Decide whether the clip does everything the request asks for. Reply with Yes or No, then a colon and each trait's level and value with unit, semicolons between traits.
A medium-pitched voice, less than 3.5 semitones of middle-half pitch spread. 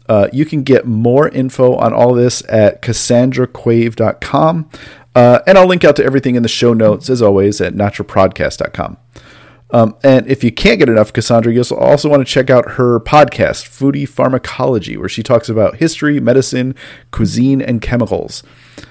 No: low, 120 Hz; average, 2.9 semitones